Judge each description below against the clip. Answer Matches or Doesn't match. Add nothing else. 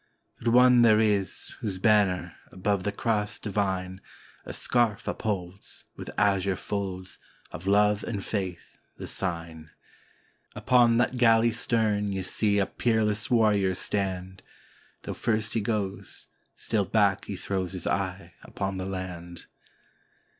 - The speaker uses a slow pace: Matches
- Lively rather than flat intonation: Doesn't match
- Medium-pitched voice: Doesn't match